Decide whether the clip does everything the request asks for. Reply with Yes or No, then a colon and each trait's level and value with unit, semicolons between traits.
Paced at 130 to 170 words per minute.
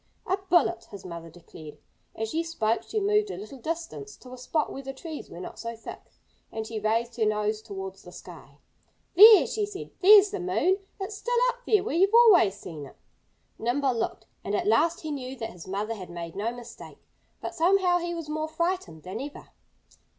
No: average, 200 wpm